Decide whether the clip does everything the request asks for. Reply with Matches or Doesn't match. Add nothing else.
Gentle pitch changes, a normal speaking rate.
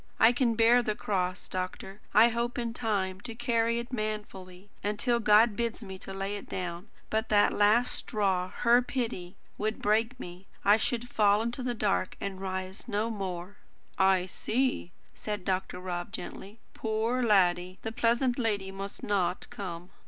Doesn't match